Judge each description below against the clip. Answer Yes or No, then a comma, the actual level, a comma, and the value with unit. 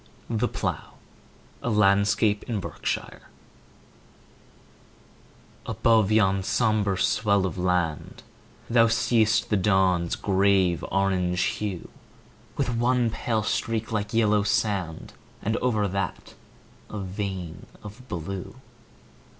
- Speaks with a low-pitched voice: Yes, low, 100 Hz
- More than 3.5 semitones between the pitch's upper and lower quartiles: No, average, 2.7 semitones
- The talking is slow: Yes, slow, 100 wpm